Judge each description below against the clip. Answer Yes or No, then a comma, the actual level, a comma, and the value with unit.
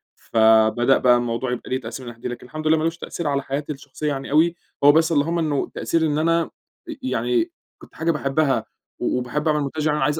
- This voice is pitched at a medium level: Yes, medium, 150 Hz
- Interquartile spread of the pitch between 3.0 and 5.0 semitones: Yes, average, 3.8 semitones